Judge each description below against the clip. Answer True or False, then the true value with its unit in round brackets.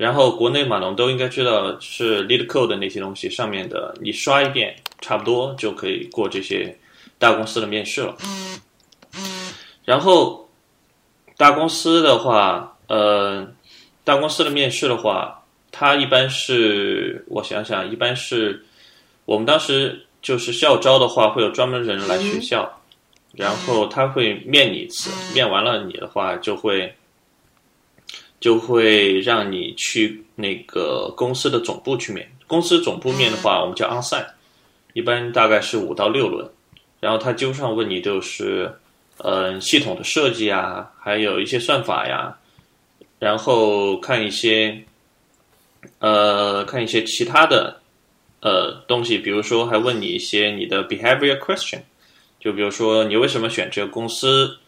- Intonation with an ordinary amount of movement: True (4.7 semitones)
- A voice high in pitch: False (125 Hz)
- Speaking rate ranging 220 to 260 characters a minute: True (250 characters per minute)